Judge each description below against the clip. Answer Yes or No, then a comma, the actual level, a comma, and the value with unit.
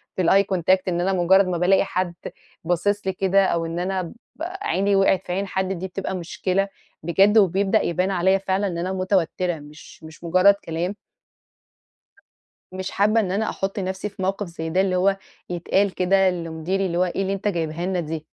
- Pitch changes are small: Yes, narrow, 2.0 semitones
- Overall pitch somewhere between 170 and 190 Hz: Yes, medium, 185 Hz